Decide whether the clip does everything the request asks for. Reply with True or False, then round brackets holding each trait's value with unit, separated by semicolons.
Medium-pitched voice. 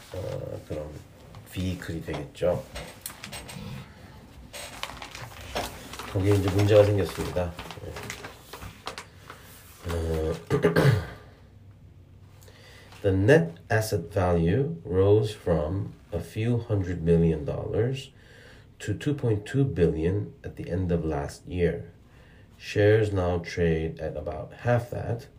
False (100 Hz)